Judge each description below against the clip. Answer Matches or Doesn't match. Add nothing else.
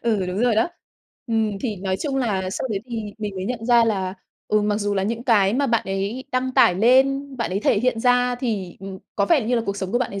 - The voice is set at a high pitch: Matches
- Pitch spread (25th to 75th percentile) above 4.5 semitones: Doesn't match